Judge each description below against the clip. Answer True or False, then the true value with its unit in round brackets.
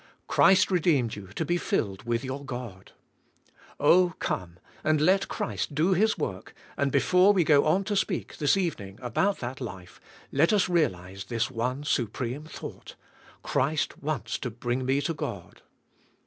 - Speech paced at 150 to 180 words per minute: True (160 wpm)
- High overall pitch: False (140 Hz)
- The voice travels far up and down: True (6.8 semitones)